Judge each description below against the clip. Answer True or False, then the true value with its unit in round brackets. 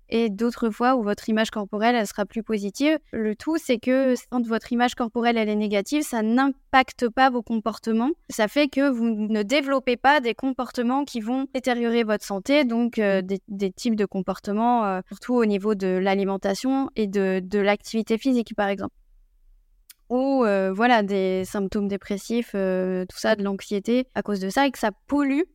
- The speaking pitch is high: True (230 Hz)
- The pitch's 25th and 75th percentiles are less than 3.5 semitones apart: False (3.8 semitones)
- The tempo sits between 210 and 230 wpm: False (190 wpm)